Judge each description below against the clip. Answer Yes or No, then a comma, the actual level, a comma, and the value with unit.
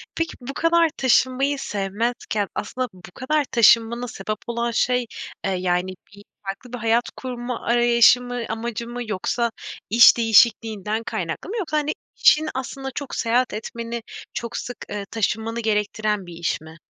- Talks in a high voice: Yes, high, 235 Hz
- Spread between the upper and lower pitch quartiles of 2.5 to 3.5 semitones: Yes, average, 3.0 semitones